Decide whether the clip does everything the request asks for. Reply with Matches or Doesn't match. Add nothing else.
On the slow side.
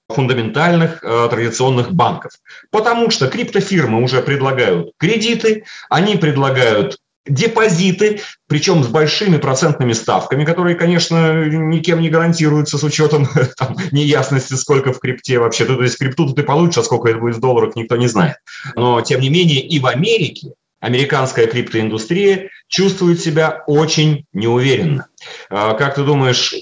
Doesn't match